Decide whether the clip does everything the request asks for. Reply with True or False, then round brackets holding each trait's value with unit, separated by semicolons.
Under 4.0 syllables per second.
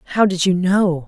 False (5.3 syllables/s)